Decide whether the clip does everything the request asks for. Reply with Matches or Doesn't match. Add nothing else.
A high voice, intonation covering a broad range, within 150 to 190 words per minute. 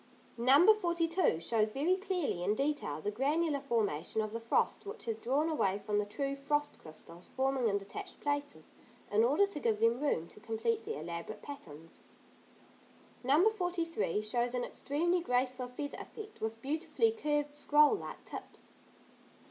Matches